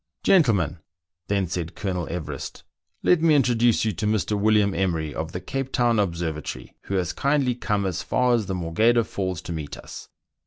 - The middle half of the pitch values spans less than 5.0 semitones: No, average, 5.3 semitones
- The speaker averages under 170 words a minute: No, average, 200 wpm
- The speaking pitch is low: Yes, low, 100 Hz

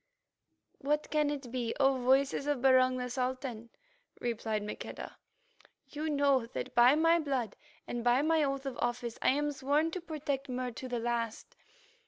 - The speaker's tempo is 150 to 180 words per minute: Yes, average, 165 wpm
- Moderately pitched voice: No, very high, 260 Hz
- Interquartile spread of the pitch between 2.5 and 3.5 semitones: Yes, average, 3.2 semitones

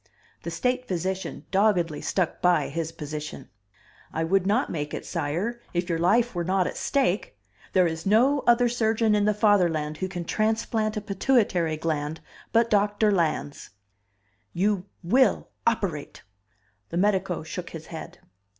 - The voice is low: No, medium, 185 Hz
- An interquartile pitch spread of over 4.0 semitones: Yes, average, 4.7 semitones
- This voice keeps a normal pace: Yes, average, 150 wpm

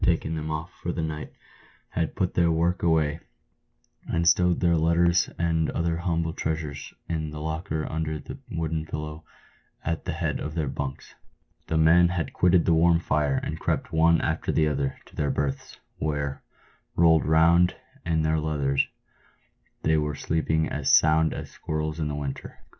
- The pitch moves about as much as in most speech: No, narrow, 1.6 semitones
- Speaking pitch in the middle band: No, very low, 80 Hz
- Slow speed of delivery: No, average, 170 wpm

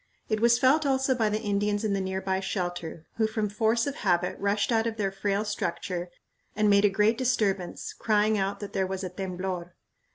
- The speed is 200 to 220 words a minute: Yes, fast, 205 wpm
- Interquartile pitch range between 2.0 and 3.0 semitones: Yes, narrow, 2.4 semitones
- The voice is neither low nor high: No, high, 205 Hz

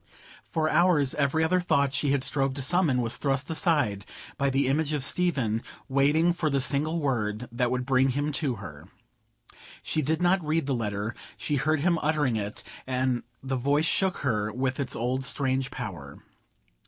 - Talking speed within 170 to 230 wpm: Yes, average, 180 wpm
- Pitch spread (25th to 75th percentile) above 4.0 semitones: No, average, 3.7 semitones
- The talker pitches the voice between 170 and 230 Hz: No, medium, 140 Hz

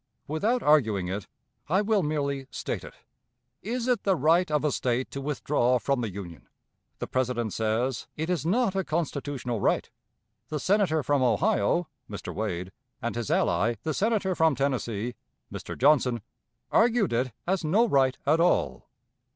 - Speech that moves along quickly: No, average, 160 wpm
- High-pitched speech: No, medium, 145 Hz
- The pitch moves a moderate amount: No, wide, 6.9 semitones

